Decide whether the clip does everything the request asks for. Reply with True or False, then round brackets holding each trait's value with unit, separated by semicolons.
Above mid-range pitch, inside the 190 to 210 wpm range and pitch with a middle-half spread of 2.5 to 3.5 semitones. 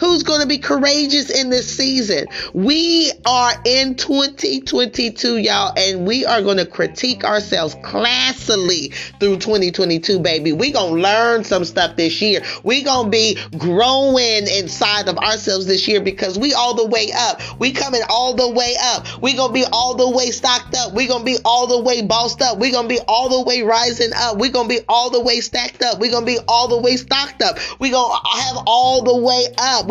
True (240 Hz; 195 wpm; 3.1 semitones)